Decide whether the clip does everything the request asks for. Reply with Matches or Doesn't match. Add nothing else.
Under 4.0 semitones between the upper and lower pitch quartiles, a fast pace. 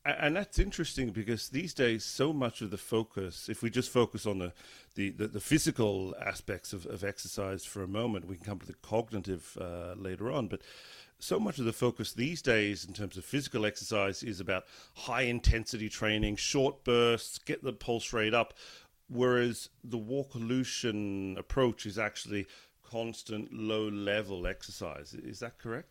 Doesn't match